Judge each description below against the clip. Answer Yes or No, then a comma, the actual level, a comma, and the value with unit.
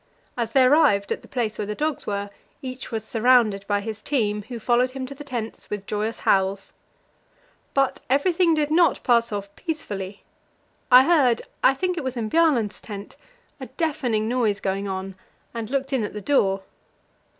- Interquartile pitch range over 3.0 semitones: Yes, average, 4.7 semitones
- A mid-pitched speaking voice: No, high, 235 Hz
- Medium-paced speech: Yes, average, 180 wpm